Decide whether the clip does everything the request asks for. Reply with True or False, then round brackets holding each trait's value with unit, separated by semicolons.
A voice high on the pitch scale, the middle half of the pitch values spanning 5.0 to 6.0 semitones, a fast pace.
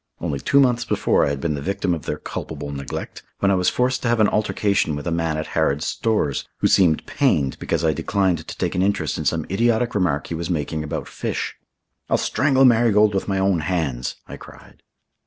False (90 Hz; 5.5 semitones; 215 wpm)